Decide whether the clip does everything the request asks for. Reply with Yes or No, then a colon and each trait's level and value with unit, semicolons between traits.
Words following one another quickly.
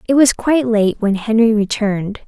No: average, 185 wpm